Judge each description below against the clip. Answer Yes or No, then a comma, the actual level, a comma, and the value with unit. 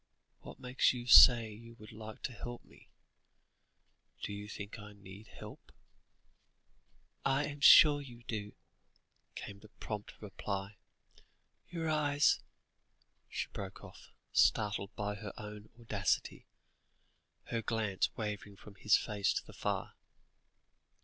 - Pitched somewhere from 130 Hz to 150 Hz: No, low, 110 Hz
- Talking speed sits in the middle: No, slow, 130 wpm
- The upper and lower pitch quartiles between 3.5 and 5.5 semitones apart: No, average, 2.8 semitones